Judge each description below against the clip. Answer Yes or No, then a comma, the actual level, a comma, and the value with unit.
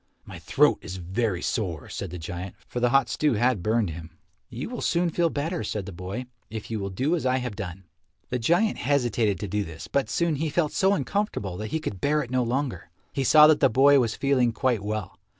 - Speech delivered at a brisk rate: Yes, fast, 230 wpm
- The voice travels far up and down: Yes, wide, 6.3 semitones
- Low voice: Yes, low, 120 Hz